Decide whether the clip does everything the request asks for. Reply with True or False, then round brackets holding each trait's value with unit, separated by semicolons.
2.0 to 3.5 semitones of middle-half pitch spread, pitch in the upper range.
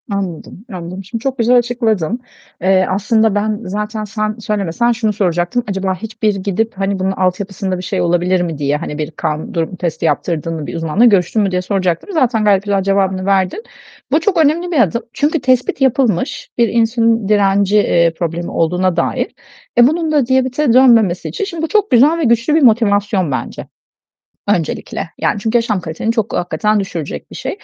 False (4.4 semitones; 205 Hz)